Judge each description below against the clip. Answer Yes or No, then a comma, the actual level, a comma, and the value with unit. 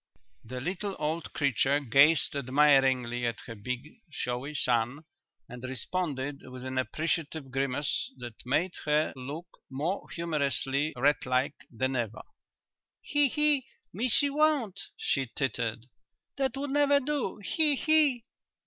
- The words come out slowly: Yes, slow, 125 wpm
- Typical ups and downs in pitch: No, wide, 6.8 semitones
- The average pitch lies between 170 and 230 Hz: No, medium, 145 Hz